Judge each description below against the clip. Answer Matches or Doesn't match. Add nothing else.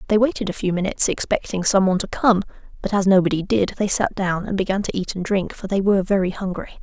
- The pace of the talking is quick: Matches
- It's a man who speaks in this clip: Doesn't match